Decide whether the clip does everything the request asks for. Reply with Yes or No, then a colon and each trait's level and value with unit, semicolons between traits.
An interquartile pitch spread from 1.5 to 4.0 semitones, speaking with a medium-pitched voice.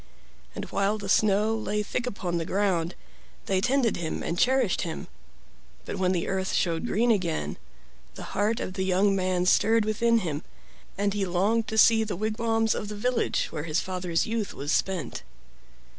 No: average, 3.5 semitones; high, 200 Hz